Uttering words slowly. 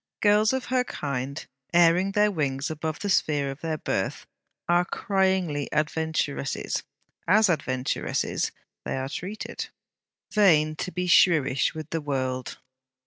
Yes: slow, 130 wpm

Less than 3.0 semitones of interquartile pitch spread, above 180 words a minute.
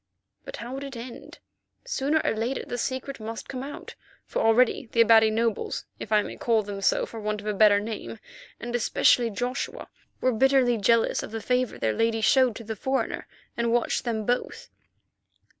Yes: narrow, 2.6 semitones; average, 190 wpm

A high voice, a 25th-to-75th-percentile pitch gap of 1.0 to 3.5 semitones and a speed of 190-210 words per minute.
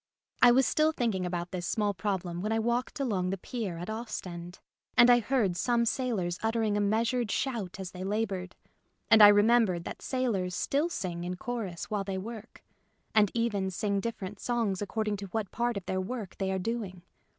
No: high, 205 Hz; average, 4.0 semitones; average, 195 wpm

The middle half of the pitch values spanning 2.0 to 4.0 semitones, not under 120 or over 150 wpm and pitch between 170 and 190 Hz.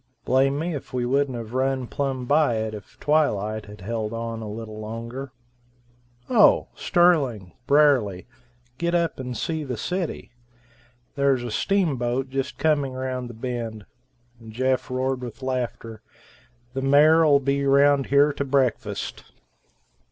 No: average, 3.6 semitones; average, 140 wpm; low, 130 Hz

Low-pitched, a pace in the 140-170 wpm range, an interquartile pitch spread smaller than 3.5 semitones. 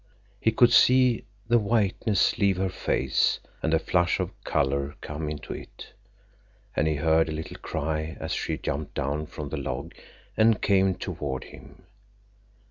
No: very low, 80 Hz; average, 160 wpm; average, 5.3 semitones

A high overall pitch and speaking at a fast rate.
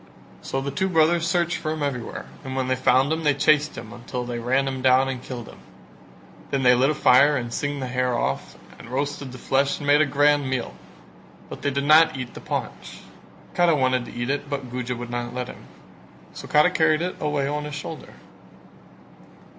No: low, 135 Hz; fast, 210 wpm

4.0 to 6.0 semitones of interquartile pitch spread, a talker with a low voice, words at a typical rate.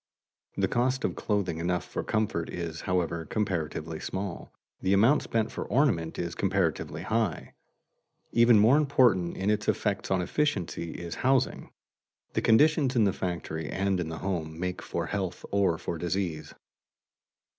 Yes: average, 4.7 semitones; very low, 95 Hz; average, 150 wpm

